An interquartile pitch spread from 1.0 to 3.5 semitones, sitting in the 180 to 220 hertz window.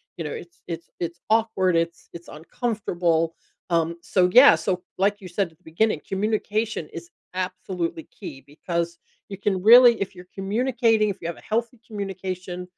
No: average, 4.2 semitones; high, 190 Hz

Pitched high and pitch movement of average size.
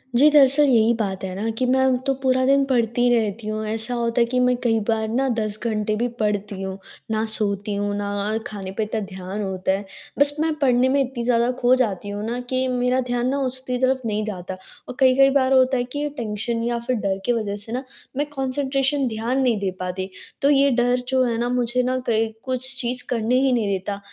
Yes: high, 235 Hz; average, 3.3 semitones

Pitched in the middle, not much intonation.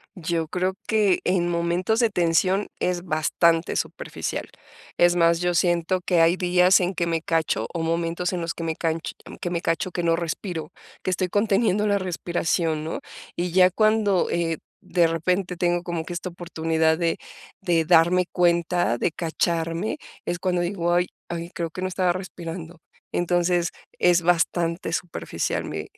Yes: medium, 175 Hz; narrow, 1.6 semitones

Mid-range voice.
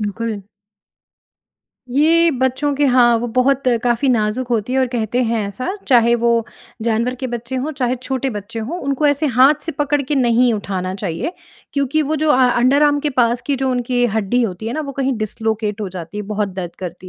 No: high, 245 Hz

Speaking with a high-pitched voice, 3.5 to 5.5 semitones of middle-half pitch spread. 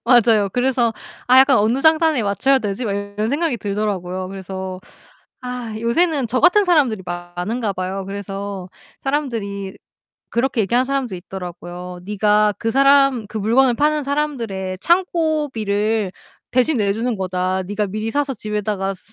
Yes: high, 220 Hz; average, 5.2 semitones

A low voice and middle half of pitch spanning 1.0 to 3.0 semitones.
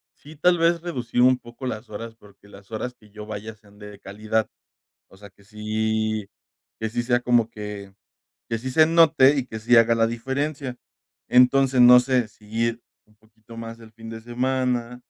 Yes: low, 115 Hz; average, 2.7 semitones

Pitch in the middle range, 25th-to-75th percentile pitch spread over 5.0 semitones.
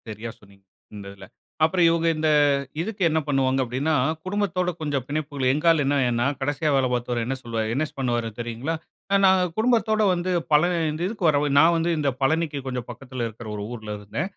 Yes: medium, 145 Hz; wide, 5.6 semitones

